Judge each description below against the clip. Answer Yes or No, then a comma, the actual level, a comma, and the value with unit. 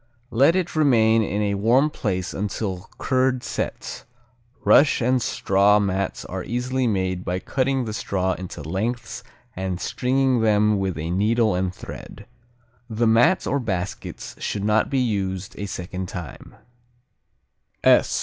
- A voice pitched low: Yes, low, 105 Hz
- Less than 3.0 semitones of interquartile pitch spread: No, average, 4.8 semitones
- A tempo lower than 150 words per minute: Yes, average, 140 wpm